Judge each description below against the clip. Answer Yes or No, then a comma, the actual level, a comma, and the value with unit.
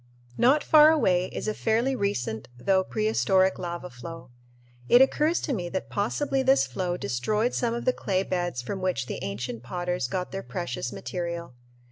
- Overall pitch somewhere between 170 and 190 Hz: Yes, medium, 185 Hz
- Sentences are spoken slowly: No, average, 170 wpm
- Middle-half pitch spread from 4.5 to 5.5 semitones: Yes, average, 5.2 semitones